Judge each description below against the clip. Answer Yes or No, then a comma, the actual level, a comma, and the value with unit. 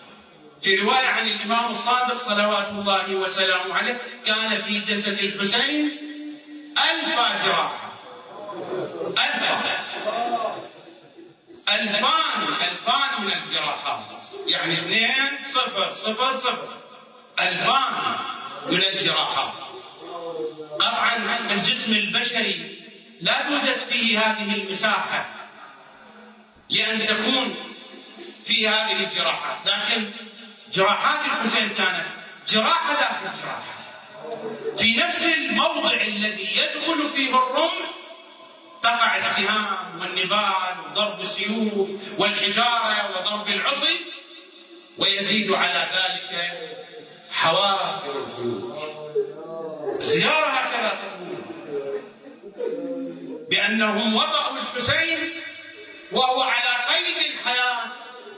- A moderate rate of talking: No, slow, 80 wpm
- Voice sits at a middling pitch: No, high, 230 Hz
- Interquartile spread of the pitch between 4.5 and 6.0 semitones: Yes, average, 5.3 semitones